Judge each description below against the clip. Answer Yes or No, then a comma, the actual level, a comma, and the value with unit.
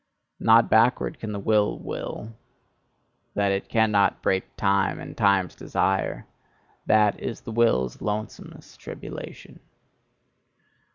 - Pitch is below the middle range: Yes, low, 105 Hz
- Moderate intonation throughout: No, narrow, 2.0 semitones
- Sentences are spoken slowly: Yes, slow, 110 wpm